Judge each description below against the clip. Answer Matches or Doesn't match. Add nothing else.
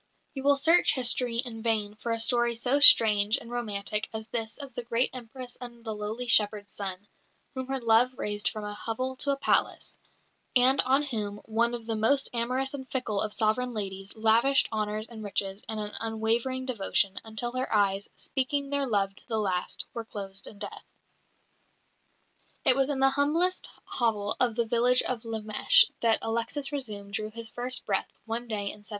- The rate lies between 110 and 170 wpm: Doesn't match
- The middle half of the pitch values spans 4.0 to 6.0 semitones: Doesn't match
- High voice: Matches